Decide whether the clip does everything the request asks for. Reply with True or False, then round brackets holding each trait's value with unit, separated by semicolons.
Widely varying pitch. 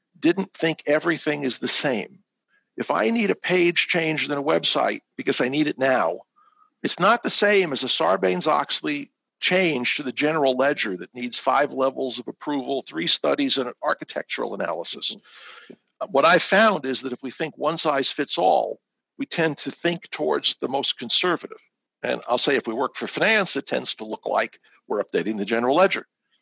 True (6.7 semitones)